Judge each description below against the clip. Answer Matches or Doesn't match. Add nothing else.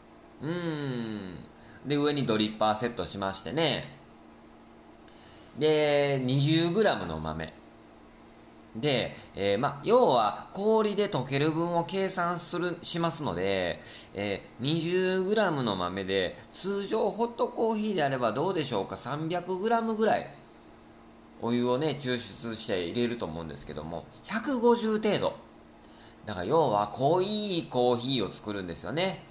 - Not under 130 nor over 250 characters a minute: Matches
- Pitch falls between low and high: Matches